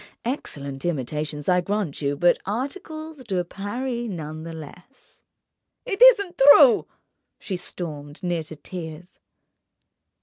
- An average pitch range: No, wide, 8.3 semitones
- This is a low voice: No, medium, 180 Hz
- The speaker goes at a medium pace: No, slow, 115 wpm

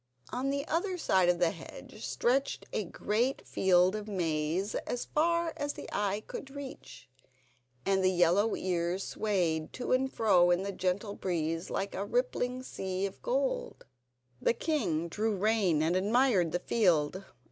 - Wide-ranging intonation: Yes, wide, 6.0 semitones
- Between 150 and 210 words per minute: Yes, average, 160 wpm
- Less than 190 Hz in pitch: No, high, 200 Hz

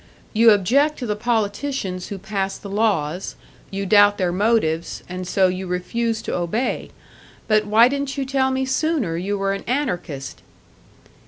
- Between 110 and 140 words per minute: No, average, 160 wpm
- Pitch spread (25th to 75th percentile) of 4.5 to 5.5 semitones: Yes, average, 4.8 semitones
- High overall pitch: Yes, high, 205 Hz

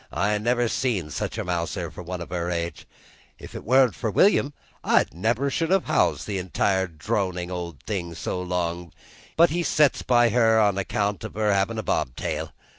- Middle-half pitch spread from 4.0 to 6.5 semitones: Yes, average, 5.3 semitones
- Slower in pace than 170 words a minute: No, average, 190 wpm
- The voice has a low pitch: Yes, low, 100 Hz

